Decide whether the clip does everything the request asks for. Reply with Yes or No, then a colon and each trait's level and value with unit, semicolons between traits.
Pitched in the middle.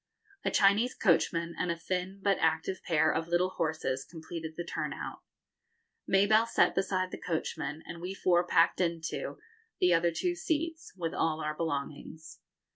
Yes: medium, 170 Hz